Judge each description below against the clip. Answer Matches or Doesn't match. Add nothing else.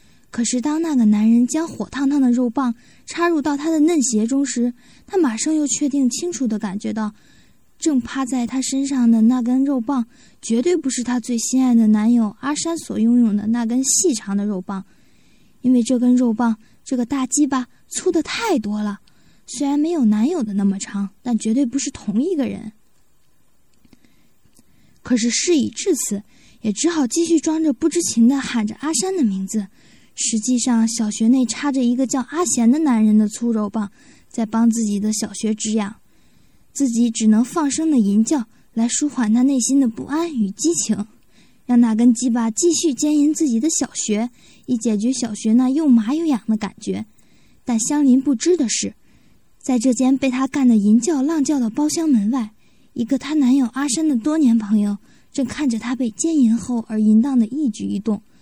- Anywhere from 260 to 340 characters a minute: Matches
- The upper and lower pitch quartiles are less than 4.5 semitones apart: Matches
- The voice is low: Doesn't match